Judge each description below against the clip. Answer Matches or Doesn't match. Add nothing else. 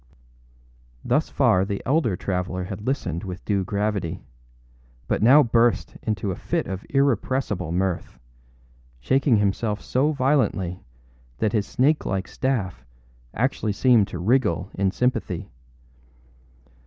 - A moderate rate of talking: Doesn't match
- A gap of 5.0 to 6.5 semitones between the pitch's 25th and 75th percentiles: Matches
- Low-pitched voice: Matches